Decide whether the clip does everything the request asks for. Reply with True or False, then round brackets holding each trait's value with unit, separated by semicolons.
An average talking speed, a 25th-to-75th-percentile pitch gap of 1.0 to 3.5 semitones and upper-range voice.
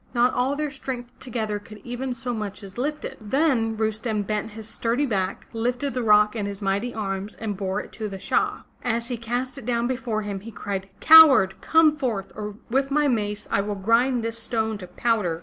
False (210 wpm; 3.2 semitones; 225 Hz)